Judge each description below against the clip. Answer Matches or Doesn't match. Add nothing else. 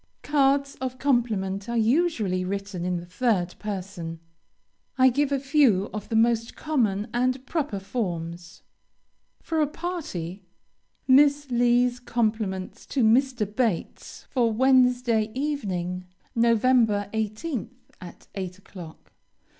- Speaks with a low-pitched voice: Doesn't match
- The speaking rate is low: Matches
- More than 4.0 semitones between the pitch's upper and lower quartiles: Matches